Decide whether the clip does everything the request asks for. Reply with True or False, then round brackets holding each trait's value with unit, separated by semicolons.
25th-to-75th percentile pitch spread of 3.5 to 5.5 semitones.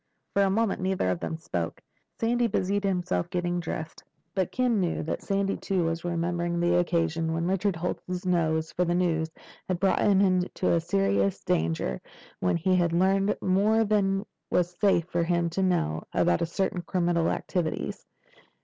False (2.7 semitones)